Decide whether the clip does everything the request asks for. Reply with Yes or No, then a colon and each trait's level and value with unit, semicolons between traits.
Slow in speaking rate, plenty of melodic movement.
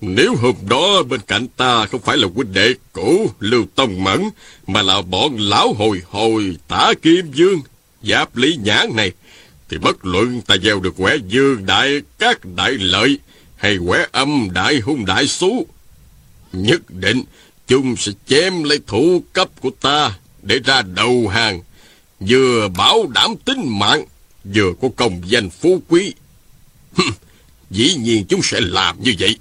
Yes: slow, 160 wpm; wide, 6.5 semitones